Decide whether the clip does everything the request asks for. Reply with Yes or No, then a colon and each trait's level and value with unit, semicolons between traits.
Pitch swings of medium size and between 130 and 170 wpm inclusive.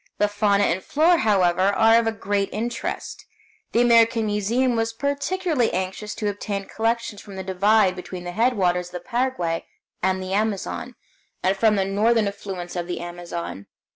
Yes: average, 3.4 semitones; average, 165 wpm